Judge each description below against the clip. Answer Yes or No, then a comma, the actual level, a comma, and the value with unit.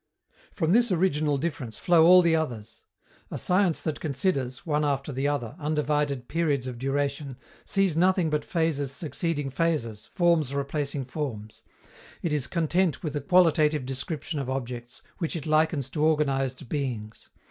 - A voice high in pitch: No, medium, 150 Hz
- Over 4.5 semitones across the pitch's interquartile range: No, average, 3.4 semitones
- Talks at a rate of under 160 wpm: Yes, average, 150 wpm